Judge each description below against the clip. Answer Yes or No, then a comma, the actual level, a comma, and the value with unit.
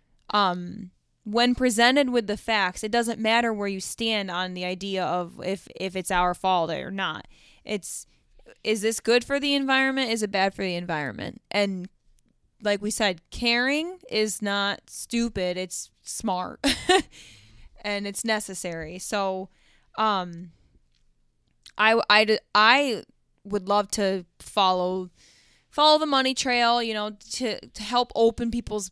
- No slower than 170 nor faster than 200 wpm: No, average, 145 wpm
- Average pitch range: Yes, average, 4.2 semitones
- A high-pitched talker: Yes, high, 205 Hz